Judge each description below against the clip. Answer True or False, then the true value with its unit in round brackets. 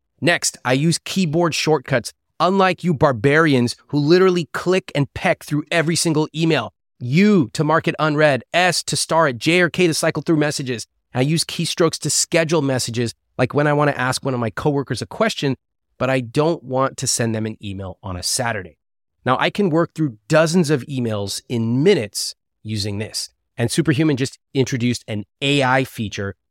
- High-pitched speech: False (140 Hz)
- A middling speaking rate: True (185 wpm)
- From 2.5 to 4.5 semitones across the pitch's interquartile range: False (5.6 semitones)